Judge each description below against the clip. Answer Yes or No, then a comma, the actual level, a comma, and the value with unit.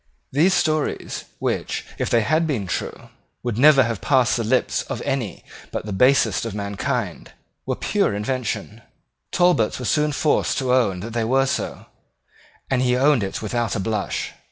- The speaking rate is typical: Yes, average, 170 wpm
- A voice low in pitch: Yes, low, 120 Hz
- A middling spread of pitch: Yes, average, 4.1 semitones